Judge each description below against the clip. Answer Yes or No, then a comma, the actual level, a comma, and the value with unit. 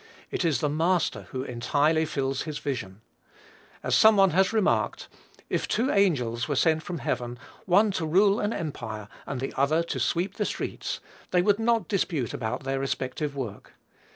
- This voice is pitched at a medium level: Yes, medium, 155 Hz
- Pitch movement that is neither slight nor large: No, wide, 6.3 semitones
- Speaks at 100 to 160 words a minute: No, average, 175 wpm